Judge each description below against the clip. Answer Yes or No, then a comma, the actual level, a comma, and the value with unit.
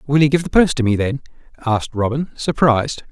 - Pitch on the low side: Yes, low, 130 Hz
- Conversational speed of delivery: No, fast, 210 wpm